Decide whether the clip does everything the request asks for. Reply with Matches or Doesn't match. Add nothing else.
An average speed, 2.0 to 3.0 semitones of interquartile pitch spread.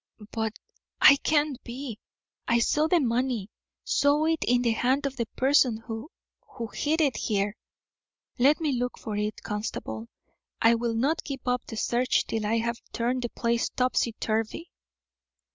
Doesn't match